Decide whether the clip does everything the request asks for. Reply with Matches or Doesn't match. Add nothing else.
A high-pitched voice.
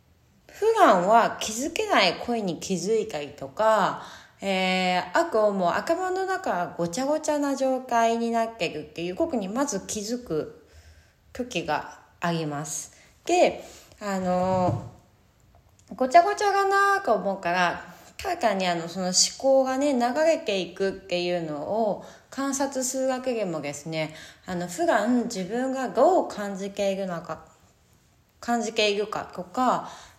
Matches